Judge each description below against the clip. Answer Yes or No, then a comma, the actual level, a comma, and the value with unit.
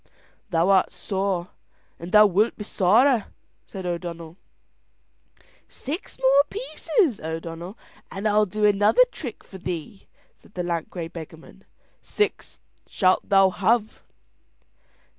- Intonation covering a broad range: No, average, 3.6 semitones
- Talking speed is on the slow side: Yes, slow, 120 wpm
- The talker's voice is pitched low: No, high, 195 Hz